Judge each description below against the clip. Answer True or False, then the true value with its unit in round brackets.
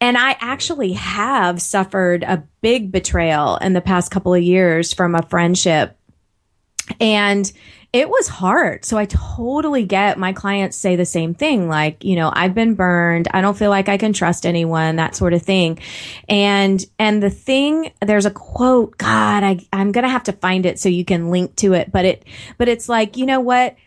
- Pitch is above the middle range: True (195 Hz)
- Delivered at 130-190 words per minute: False (200 wpm)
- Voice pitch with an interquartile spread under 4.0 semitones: True (3.5 semitones)